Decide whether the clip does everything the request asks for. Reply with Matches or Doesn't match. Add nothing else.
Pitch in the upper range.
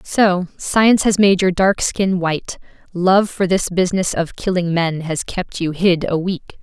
Doesn't match